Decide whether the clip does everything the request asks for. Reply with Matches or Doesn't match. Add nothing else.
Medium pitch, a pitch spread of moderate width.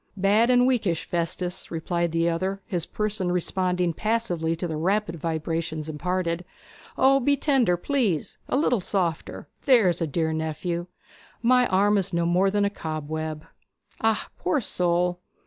Matches